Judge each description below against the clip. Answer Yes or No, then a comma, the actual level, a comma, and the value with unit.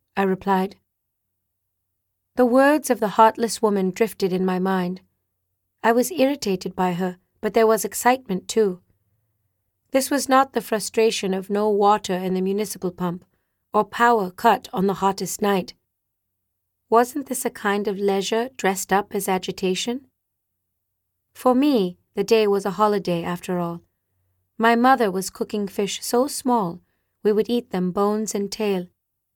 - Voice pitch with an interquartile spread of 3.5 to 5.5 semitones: Yes, average, 4.7 semitones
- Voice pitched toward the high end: Yes, high, 195 Hz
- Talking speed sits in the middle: Yes, average, 150 wpm